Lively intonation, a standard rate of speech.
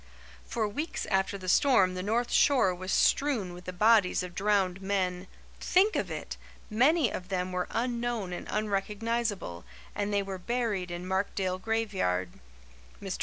No: average, 3.9 semitones; average, 155 wpm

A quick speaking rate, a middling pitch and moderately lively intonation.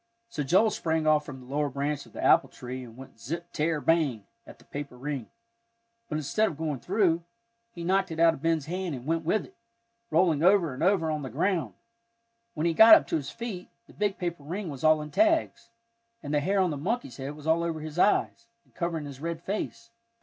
Yes: fast, 225 wpm; medium, 160 Hz; average, 3.9 semitones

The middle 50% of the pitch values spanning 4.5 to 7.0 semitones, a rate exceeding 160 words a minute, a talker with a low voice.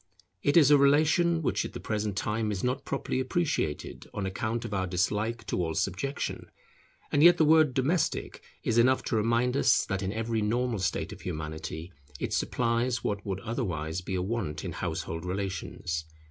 Yes: wide, 5.6 semitones; average, 180 wpm; low, 110 Hz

